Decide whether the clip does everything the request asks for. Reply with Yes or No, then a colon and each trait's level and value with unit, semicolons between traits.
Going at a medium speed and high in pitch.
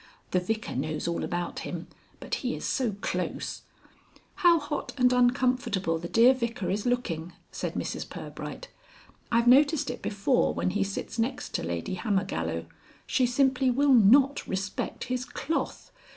Yes: average, 155 wpm; high, 235 Hz